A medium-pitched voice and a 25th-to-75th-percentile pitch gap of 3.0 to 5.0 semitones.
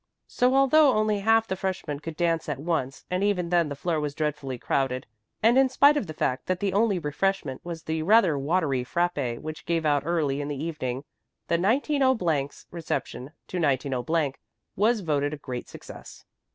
No: medium, 165 Hz; wide, 5.4 semitones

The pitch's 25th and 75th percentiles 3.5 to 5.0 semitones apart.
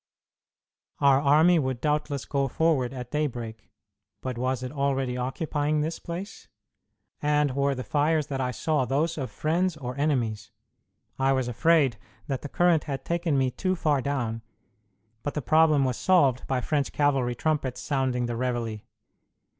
No: average, 3.1 semitones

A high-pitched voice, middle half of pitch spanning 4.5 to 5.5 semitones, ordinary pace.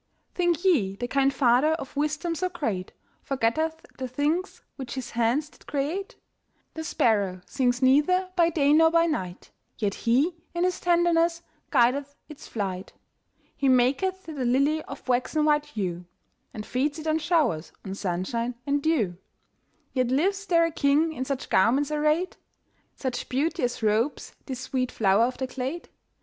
Yes: very high, 280 Hz; average, 4.8 semitones; average, 160 wpm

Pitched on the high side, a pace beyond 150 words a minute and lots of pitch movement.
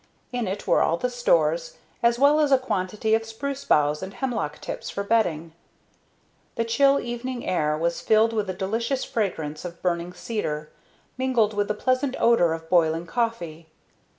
Yes: high, 215 Hz; average, 170 wpm; wide, 6.3 semitones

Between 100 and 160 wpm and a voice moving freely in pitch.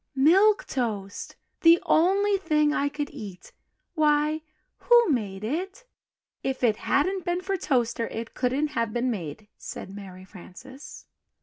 Yes: slow, 135 wpm; wide, 7.5 semitones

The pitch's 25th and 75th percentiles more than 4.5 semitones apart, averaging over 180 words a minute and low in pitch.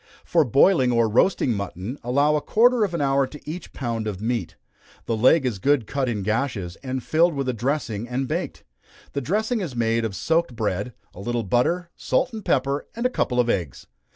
Yes: average, 5.1 semitones; fast, 205 wpm; low, 130 Hz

